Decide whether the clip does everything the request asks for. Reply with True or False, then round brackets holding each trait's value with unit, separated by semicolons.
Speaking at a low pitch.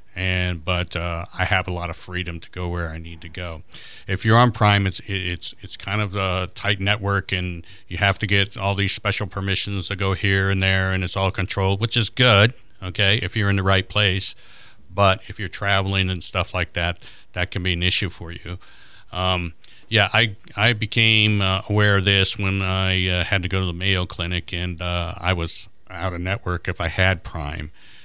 True (95 Hz)